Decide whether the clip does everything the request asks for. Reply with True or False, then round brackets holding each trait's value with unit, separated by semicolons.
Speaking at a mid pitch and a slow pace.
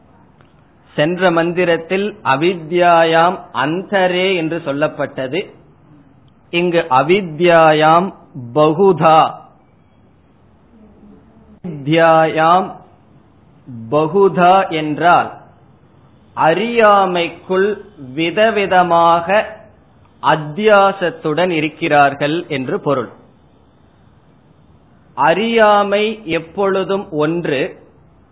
True (170 Hz; 45 wpm)